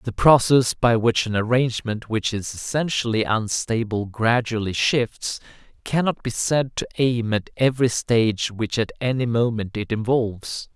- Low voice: Yes, low, 115 Hz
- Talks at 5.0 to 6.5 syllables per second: No, 4.5 syllables/s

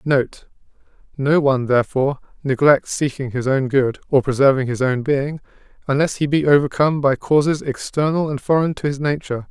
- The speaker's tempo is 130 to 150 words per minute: No, average, 160 wpm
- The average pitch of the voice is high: No, medium, 140 Hz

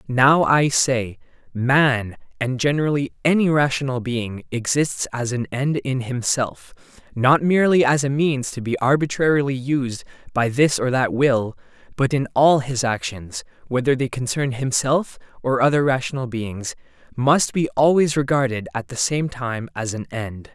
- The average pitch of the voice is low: Yes, low, 130 Hz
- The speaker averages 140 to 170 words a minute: Yes, average, 155 wpm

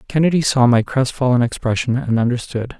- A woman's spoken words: No, male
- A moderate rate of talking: Yes, average, 150 wpm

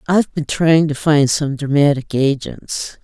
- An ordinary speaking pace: Yes, average, 160 wpm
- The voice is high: No, medium, 145 Hz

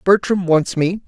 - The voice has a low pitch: No, medium, 185 Hz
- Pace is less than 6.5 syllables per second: Yes, 4.3 syllables/s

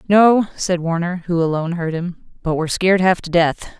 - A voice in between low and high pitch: Yes, medium, 175 Hz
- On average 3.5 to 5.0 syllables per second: No, 5.5 syllables/s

